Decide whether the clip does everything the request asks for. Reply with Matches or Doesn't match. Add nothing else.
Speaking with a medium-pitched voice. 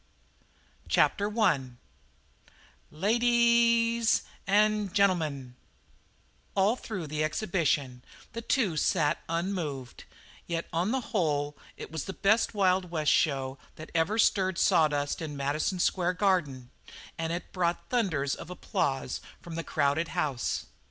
Matches